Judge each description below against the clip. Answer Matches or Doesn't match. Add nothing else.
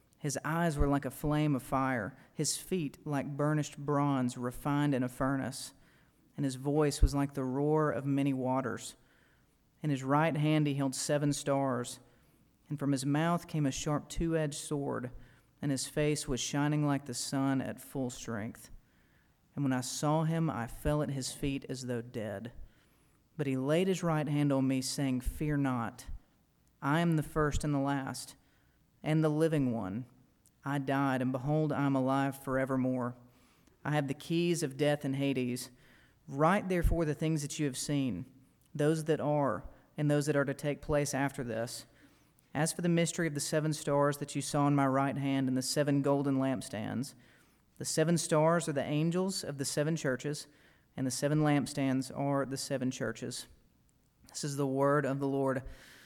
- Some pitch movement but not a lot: Doesn't match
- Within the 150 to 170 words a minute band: Doesn't match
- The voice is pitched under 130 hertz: Doesn't match